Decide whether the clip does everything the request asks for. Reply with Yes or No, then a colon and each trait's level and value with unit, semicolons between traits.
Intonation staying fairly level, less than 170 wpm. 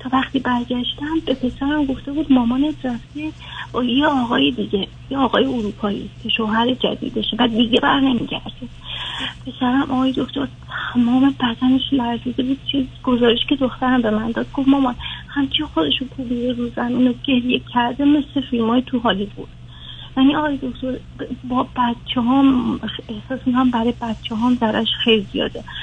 Yes: narrow, 2.1 semitones; average, 150 wpm